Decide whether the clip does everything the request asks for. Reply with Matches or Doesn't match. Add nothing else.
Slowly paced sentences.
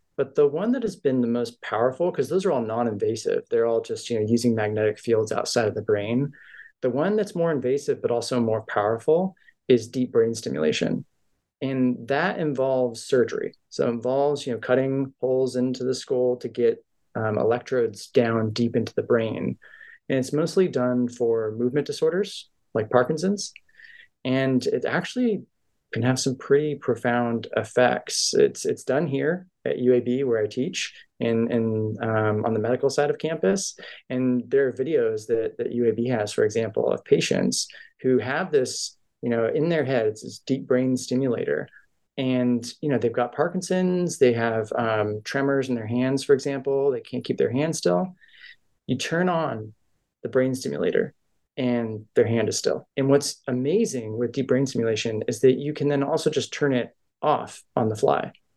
Doesn't match